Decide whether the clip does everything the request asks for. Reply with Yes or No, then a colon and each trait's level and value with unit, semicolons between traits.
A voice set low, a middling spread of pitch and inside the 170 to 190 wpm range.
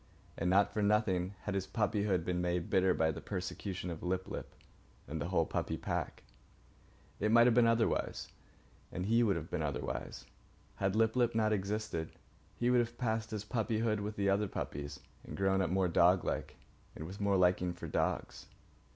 Yes: low, 100 Hz; average, 3.4 semitones; average, 185 wpm